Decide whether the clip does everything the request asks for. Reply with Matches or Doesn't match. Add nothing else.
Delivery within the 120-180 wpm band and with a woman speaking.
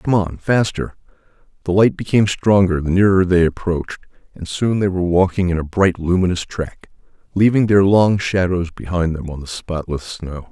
Doesn't match